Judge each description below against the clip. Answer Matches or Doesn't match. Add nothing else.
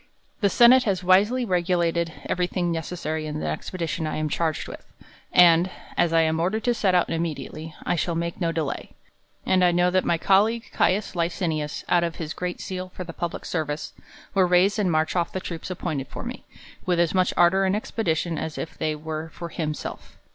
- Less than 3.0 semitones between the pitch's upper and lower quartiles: Matches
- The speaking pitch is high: Doesn't match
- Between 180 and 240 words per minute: Matches